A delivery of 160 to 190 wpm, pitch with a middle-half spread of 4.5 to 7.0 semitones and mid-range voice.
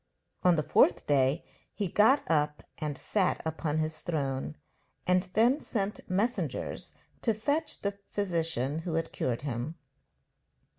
No: slow, 135 wpm; wide, 5.4 semitones; medium, 165 Hz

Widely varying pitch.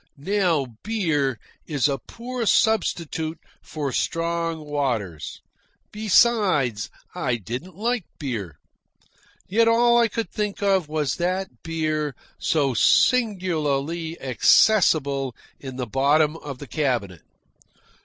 Yes: wide, 6.2 semitones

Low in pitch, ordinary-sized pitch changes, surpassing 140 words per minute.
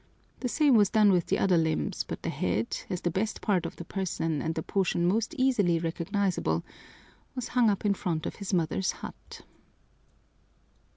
No: medium, 185 Hz; average, 4.1 semitones; average, 180 wpm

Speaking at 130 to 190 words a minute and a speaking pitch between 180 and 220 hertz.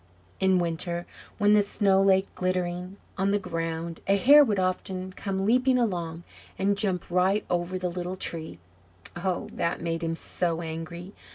Yes: average, 160 wpm; medium, 185 Hz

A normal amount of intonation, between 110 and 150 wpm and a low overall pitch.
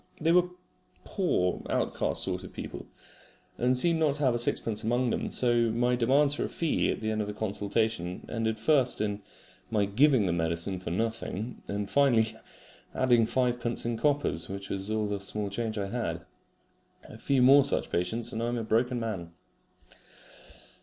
No: average, 3.6 semitones; average, 175 wpm; low, 115 Hz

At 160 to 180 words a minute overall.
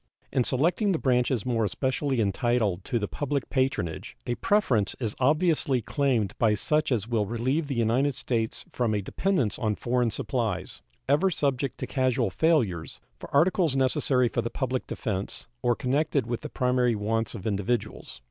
Yes: average, 165 wpm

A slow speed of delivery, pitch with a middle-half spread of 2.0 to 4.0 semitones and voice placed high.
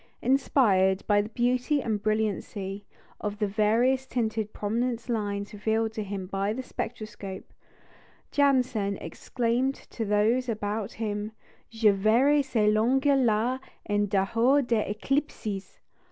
Yes: slow, 125 wpm; average, 3.3 semitones; high, 220 Hz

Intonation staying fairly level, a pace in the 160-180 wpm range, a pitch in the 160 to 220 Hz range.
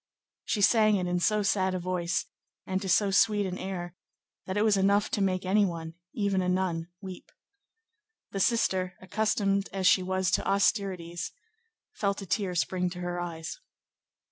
Yes: narrow, 2.0 semitones; average, 170 wpm; high, 190 Hz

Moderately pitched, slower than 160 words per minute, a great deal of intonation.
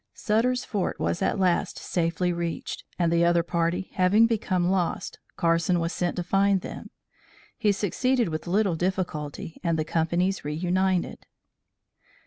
No: medium, 180 Hz; average, 140 wpm; narrow, 2.4 semitones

